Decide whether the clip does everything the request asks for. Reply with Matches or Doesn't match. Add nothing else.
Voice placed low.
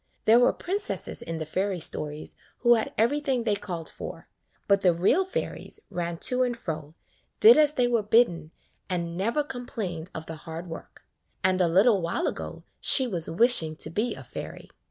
Doesn't match